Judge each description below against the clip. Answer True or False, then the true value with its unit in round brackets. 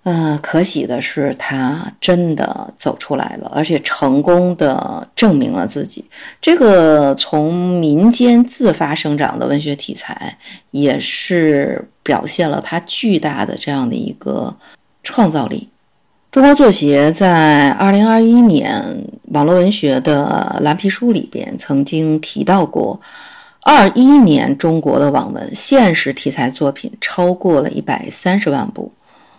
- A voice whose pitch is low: False (175 Hz)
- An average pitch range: False (8.0 semitones)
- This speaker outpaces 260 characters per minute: False (205 characters per minute)